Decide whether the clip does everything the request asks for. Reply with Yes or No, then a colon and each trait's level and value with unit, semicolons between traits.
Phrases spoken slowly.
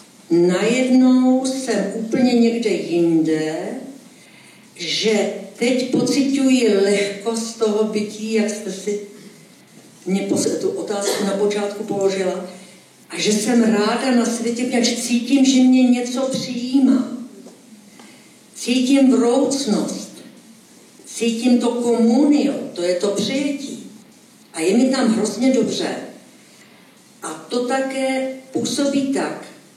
Yes: slow, 105 wpm